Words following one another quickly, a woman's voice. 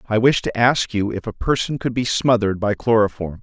No: fast, 230 wpm; male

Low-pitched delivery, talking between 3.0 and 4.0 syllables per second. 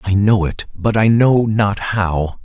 Yes: low, 100 Hz; 3.6 syllables/s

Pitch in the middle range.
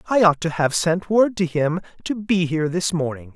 Yes: medium, 170 Hz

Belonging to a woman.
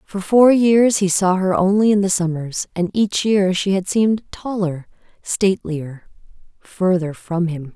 Yes: female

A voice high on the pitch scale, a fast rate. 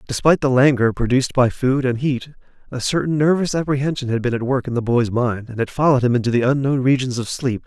No: low, 130 Hz; fast, 235 wpm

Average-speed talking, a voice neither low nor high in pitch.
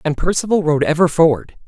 Yes: average, 180 wpm; medium, 160 Hz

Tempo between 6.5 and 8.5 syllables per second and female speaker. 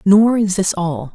No: 3.8 syllables/s; female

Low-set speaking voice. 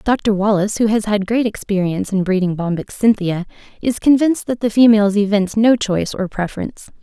No: high, 210 Hz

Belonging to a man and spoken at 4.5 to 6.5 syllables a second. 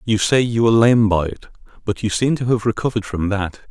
Yes: male; 6.2 syllables/s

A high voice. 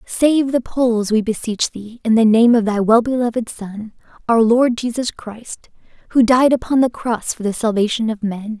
Yes: high, 230 Hz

